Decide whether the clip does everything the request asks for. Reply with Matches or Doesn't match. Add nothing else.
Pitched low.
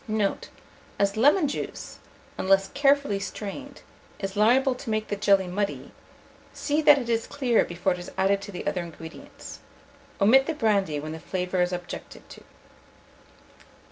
Doesn't match